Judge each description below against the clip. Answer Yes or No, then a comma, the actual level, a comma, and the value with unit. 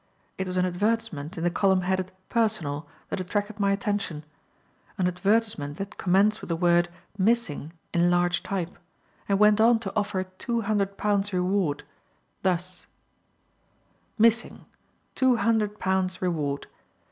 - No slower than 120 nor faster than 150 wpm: Yes, slow, 135 wpm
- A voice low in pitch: No, high, 190 Hz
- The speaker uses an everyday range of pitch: Yes, average, 3.0 semitones